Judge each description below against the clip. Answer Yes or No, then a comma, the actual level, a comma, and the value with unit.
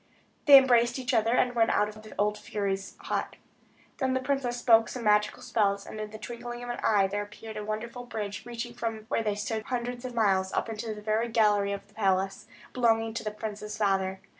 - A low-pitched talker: No, high, 220 Hz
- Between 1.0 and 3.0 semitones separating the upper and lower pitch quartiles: Yes, narrow, 2.5 semitones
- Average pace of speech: No, fast, 215 wpm